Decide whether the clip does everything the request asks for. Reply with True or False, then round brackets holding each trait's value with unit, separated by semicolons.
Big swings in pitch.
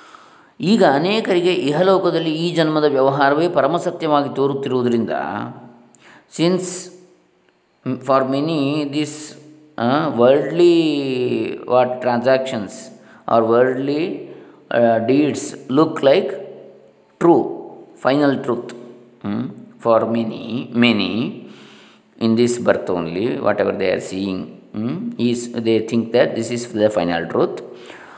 True (6.2 semitones)